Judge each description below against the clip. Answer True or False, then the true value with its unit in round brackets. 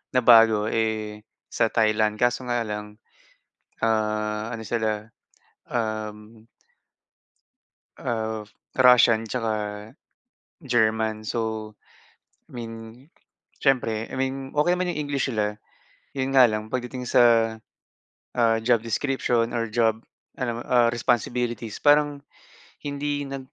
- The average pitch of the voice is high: False (115 Hz)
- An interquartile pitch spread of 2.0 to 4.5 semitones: True (2.5 semitones)